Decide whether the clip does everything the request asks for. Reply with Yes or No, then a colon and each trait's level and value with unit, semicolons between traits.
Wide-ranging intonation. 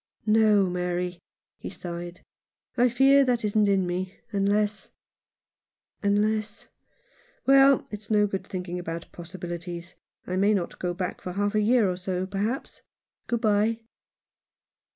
No: average, 3.1 semitones